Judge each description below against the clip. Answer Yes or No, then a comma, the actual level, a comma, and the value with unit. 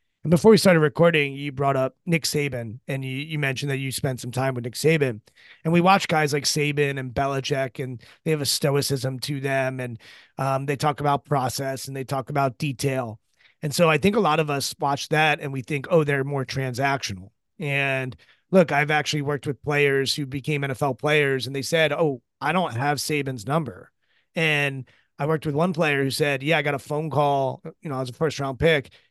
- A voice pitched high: No, medium, 140 Hz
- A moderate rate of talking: No, fast, 215 wpm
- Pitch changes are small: Yes, narrow, 2.2 semitones